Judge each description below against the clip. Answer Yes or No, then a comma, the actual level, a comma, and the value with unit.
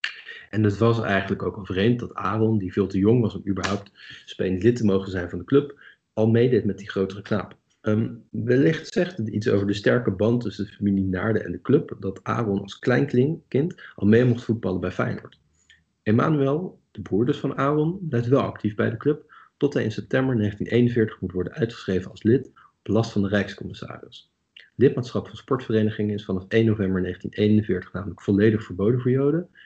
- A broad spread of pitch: No, average, 3.7 semitones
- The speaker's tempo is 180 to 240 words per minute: Yes, average, 195 wpm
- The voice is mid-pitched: No, low, 110 Hz